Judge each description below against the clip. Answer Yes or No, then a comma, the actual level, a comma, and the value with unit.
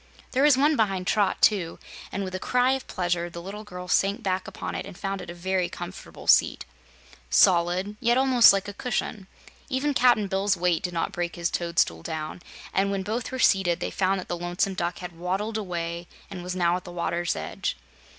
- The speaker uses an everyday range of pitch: Yes, average, 3.0 semitones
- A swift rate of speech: Yes, fast, 210 wpm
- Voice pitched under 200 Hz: Yes, medium, 185 Hz